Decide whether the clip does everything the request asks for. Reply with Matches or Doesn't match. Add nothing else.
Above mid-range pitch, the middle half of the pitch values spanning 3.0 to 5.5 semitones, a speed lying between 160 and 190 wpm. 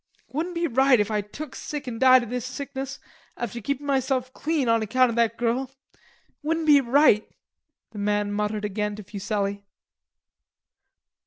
Matches